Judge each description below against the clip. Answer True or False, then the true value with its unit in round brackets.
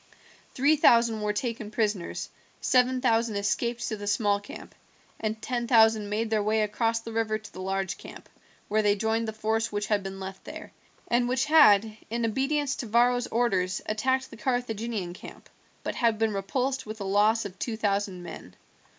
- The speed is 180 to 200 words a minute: True (185 wpm)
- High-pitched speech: True (220 Hz)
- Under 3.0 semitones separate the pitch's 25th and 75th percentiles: True (2.5 semitones)